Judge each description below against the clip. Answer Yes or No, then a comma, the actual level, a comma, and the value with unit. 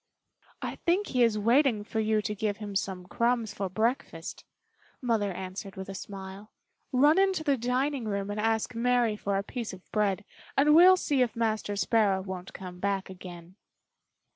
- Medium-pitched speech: No, high, 215 Hz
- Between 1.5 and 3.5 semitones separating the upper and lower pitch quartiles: No, average, 4.1 semitones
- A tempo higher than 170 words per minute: Yes, average, 180 wpm